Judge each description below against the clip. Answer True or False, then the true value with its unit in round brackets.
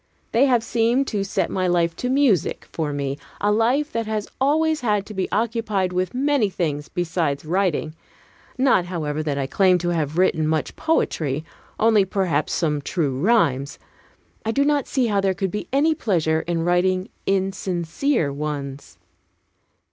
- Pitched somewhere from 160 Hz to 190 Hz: True (185 Hz)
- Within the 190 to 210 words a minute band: False (165 wpm)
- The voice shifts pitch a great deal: True (6.3 semitones)